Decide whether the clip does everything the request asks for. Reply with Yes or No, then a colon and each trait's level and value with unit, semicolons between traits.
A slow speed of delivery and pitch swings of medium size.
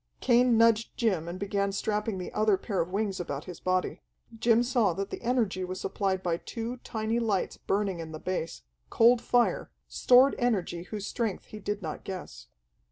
No: average, 180 wpm; average, 3.8 semitones